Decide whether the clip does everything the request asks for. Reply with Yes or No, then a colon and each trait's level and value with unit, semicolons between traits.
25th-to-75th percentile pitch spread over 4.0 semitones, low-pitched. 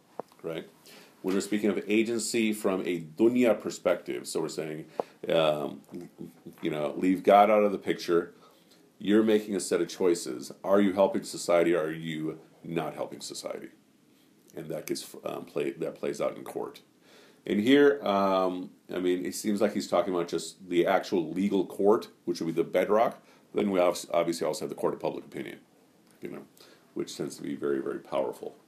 No: average, 3.7 semitones; very low, 95 Hz